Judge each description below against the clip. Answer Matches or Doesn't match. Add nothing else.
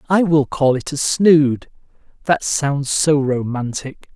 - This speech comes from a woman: Doesn't match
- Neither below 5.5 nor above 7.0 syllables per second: Doesn't match